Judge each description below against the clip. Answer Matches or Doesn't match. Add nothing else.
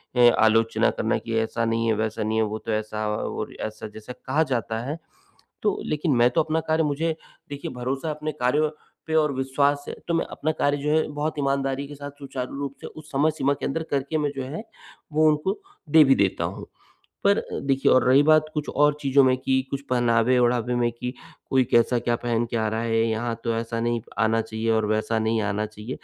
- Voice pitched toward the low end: Matches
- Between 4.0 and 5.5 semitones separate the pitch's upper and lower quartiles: Matches